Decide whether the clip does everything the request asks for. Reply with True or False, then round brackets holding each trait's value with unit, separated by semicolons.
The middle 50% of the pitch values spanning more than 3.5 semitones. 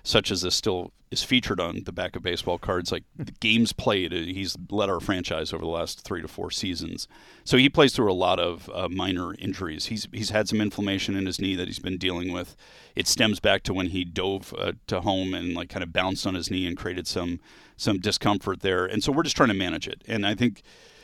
False (2.9 semitones)